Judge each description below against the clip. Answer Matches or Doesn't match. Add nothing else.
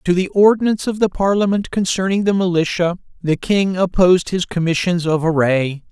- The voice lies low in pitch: Doesn't match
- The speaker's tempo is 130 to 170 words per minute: Matches